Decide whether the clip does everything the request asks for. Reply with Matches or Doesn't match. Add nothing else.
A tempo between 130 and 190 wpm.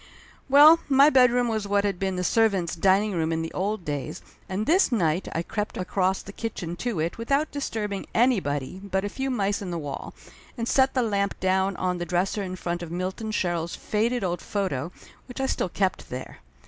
Doesn't match